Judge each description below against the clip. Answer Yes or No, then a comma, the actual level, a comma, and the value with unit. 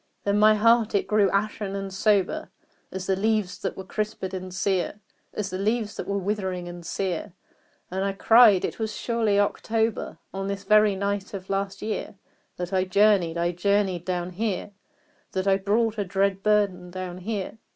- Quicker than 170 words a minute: Yes, average, 180 wpm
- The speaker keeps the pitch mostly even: Yes, narrow, 2.1 semitones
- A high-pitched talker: Yes, high, 195 Hz